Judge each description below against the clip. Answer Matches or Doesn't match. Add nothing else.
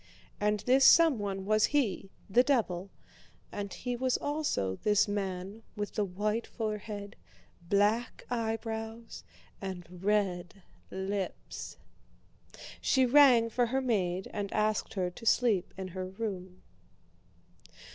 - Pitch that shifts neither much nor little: Matches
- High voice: Matches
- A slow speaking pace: Matches